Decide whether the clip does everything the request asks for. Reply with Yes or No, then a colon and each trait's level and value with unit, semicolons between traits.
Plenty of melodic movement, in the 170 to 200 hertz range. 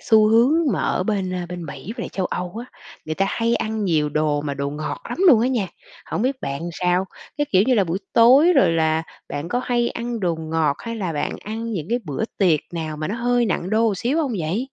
Yes: wide, 6.3 semitones; high, 195 Hz